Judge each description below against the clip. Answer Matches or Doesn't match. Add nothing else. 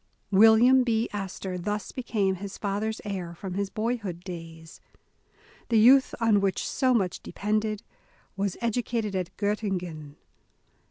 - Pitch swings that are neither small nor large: Matches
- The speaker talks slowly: Matches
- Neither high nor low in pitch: Doesn't match